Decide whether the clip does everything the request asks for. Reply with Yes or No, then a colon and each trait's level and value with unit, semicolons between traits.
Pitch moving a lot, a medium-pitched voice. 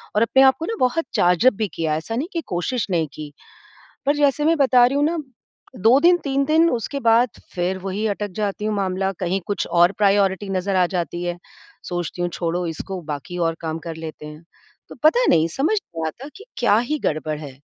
No: wide, 7.5 semitones; high, 195 Hz